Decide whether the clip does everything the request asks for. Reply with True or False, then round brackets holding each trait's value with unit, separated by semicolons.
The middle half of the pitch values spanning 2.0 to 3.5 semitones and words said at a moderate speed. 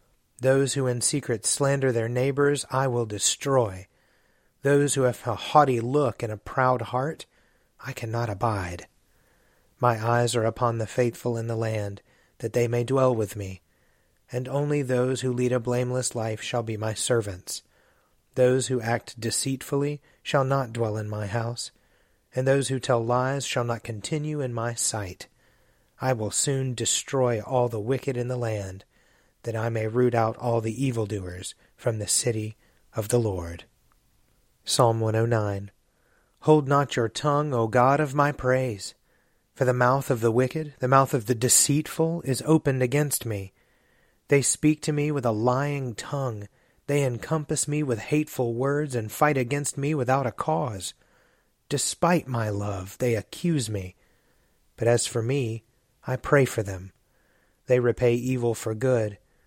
True (3.2 semitones; 160 wpm)